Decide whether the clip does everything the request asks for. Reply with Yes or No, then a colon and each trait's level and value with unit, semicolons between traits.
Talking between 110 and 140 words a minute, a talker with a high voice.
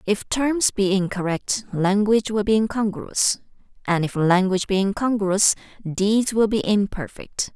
Yes: slow, 135 wpm; high, 200 Hz